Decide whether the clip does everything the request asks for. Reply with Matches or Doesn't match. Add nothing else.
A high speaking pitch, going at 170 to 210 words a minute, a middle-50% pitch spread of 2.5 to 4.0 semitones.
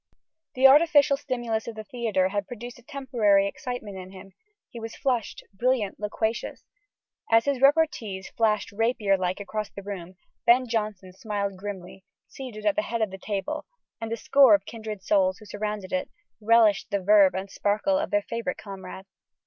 Matches